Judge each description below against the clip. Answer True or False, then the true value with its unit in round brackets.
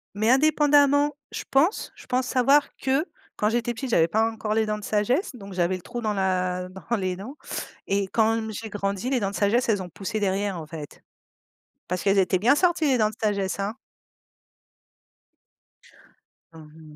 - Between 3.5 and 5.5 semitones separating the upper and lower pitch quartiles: True (4.5 semitones)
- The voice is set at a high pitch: True (210 Hz)